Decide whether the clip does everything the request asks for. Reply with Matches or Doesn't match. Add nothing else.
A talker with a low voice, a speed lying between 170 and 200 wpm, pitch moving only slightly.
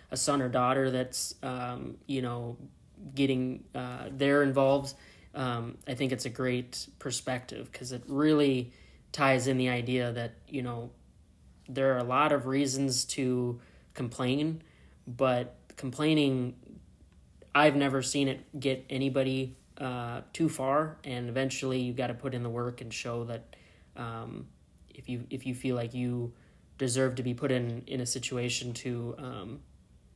Doesn't match